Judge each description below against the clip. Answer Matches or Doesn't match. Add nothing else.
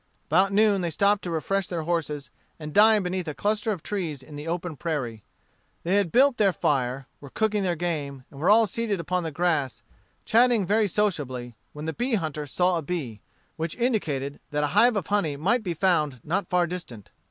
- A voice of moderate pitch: Matches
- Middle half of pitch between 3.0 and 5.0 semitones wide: Doesn't match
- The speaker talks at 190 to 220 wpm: Matches